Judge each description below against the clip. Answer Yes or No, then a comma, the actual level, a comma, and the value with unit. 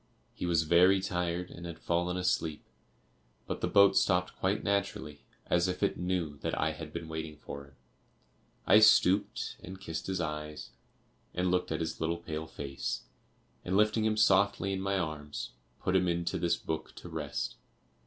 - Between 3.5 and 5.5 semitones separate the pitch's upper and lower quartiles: No, average, 3.0 semitones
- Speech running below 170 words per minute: No, average, 175 wpm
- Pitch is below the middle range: Yes, very low, 85 Hz